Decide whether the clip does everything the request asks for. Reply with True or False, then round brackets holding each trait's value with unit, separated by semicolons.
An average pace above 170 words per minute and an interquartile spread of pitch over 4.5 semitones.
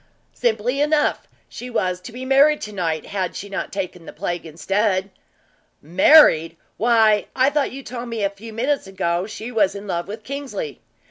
True (180 wpm; 5.0 semitones)